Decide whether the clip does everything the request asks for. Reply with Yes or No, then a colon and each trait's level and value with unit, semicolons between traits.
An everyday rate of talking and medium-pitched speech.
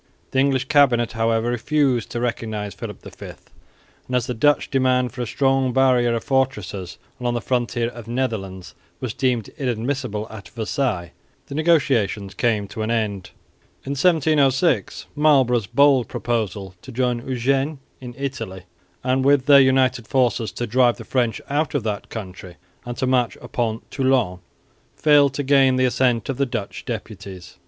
No: average, 165 wpm; low, 125 Hz